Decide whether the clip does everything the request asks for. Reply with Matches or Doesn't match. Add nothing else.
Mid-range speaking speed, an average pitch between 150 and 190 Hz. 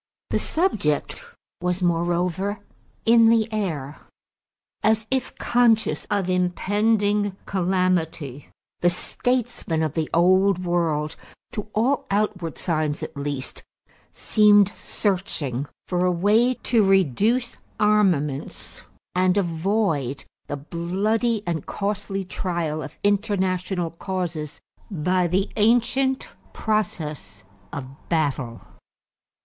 Doesn't match